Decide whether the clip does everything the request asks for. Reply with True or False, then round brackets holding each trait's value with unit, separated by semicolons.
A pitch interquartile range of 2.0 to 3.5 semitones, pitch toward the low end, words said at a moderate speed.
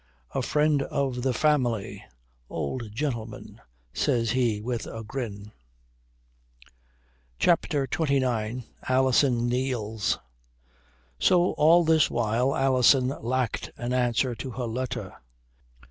False (2.8 semitones; 125 Hz; 100 wpm)